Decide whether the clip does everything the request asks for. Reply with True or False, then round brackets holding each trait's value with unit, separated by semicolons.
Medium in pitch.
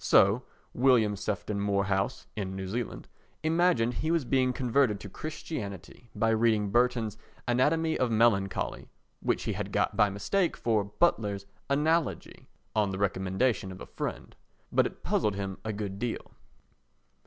False (110 Hz)